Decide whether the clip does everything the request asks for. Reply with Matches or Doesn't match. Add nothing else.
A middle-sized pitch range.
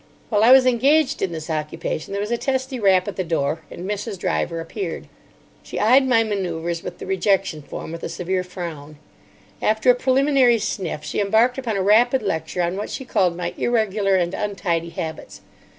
Doesn't match